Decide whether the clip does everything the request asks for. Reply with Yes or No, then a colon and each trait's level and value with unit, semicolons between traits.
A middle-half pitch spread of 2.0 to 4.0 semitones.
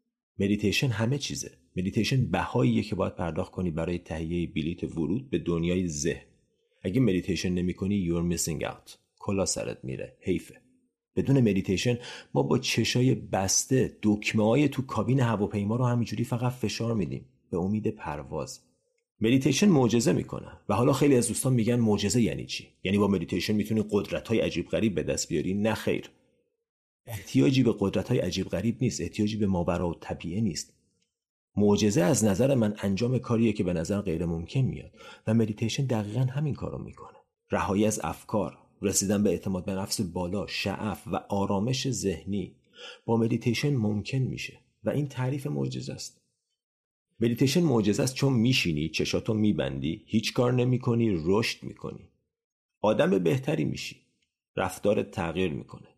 No: average, 4.6 semitones